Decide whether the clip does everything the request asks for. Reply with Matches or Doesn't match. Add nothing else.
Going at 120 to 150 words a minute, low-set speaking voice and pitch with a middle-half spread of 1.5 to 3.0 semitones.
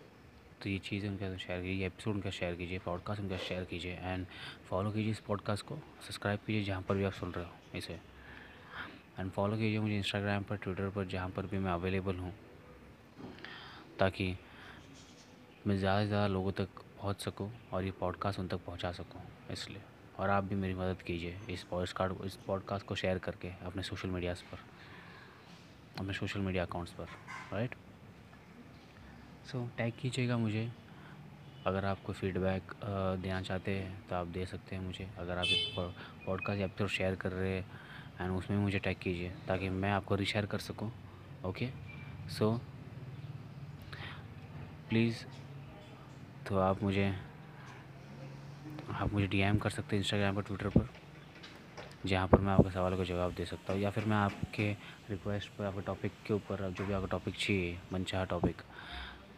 Doesn't match